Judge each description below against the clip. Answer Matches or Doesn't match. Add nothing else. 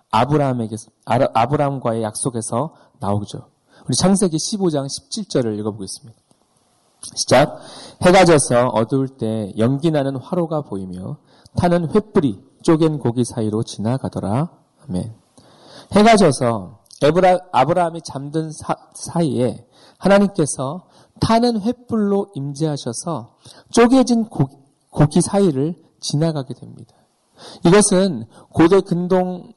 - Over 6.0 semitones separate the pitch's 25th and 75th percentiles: Matches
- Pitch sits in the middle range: Matches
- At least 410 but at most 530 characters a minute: Doesn't match